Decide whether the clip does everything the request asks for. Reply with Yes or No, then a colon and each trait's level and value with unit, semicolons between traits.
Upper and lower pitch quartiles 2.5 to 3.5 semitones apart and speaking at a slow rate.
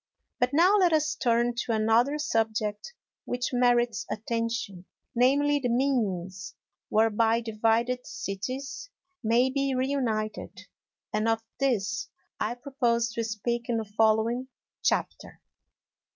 Yes: average, 2.8 semitones; slow, 115 wpm